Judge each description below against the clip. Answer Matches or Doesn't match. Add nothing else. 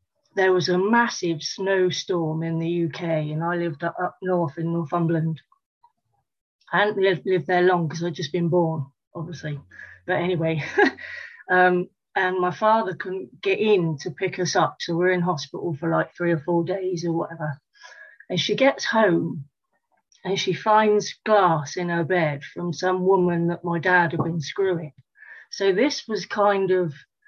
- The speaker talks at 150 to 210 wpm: Matches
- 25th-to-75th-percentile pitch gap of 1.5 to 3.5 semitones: Matches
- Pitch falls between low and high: Matches